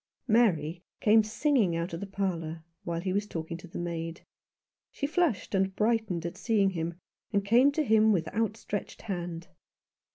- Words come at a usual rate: Yes, average, 165 wpm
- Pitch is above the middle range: Yes, high, 195 Hz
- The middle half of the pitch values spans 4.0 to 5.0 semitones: Yes, average, 4.6 semitones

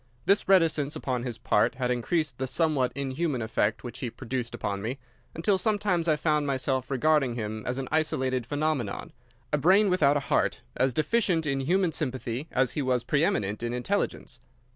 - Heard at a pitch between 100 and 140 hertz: Yes, low, 135 Hz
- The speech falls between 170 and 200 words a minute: Yes, average, 180 wpm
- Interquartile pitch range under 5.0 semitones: Yes, average, 4.2 semitones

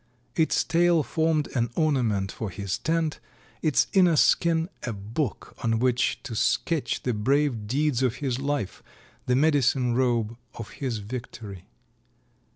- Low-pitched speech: Yes, low, 130 Hz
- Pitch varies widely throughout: No, average, 5.0 semitones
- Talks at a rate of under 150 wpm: Yes, average, 140 wpm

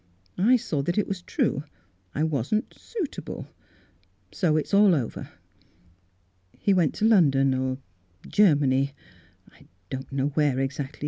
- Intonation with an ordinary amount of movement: No, wide, 6.1 semitones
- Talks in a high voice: No, medium, 145 Hz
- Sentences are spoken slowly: No, average, 145 wpm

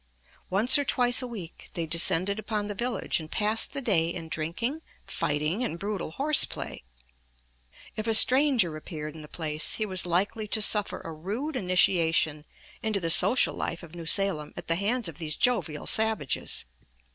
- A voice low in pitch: No, high, 190 Hz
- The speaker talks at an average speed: Yes, average, 175 wpm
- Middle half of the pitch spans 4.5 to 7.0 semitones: Yes, wide, 5.5 semitones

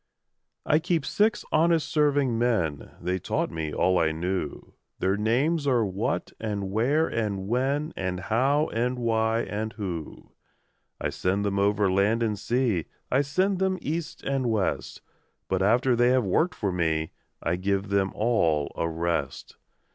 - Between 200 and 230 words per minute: No, average, 155 wpm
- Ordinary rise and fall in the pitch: No, wide, 6.1 semitones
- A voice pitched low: Yes, low, 110 Hz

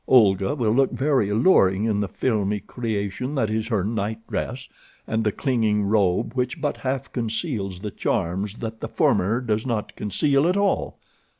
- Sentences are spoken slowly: No, average, 170 wpm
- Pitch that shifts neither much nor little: Yes, average, 3.9 semitones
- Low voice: Yes, low, 110 Hz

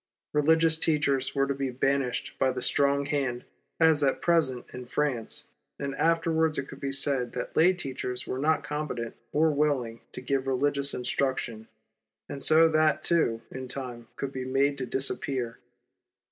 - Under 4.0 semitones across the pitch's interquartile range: Yes, average, 2.9 semitones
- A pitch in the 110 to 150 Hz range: Yes, medium, 140 Hz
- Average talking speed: Yes, average, 160 wpm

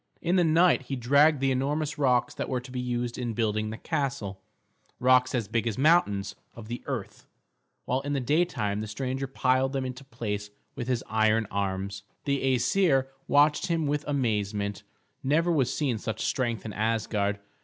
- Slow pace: No, average, 175 wpm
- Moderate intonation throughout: Yes, average, 4.3 semitones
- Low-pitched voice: Yes, low, 125 Hz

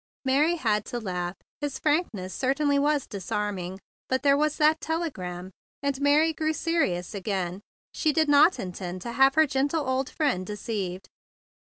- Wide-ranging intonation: Yes, wide, 7.9 semitones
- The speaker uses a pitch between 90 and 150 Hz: No, very high, 265 Hz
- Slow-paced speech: No, average, 155 wpm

